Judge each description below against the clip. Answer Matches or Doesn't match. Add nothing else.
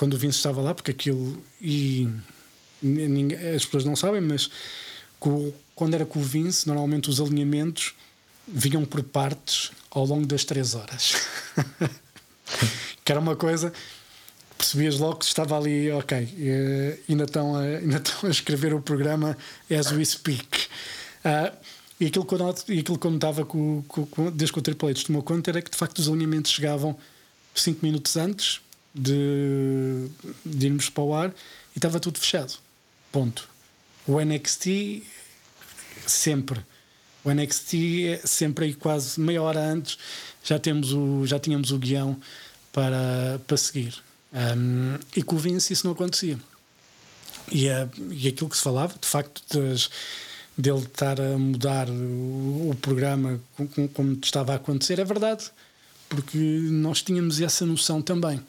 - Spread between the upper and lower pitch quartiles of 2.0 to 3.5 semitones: Matches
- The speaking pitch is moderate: Matches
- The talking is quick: Doesn't match